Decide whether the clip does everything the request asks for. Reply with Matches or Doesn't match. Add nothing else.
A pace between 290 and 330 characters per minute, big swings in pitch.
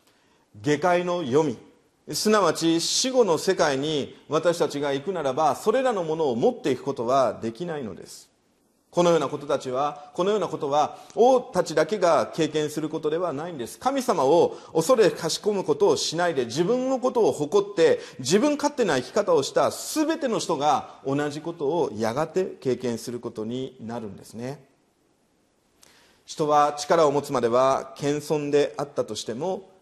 Matches